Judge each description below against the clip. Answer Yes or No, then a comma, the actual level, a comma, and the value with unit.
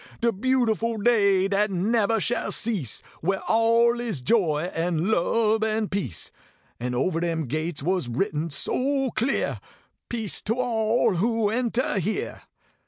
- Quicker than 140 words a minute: No, slow, 135 wpm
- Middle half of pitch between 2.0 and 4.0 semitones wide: No, average, 5.0 semitones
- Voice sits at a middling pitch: No, high, 210 Hz